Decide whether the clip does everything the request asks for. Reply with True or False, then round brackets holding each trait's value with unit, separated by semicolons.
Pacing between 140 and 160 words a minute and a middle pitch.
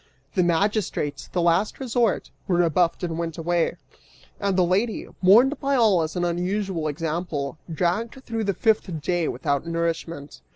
True (155 wpm; 175 Hz)